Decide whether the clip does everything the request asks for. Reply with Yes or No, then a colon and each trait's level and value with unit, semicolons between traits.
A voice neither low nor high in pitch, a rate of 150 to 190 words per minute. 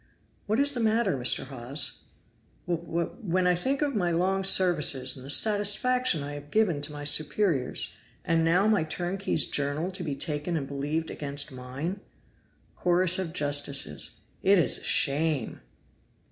Yes: medium, 165 Hz; average, 160 wpm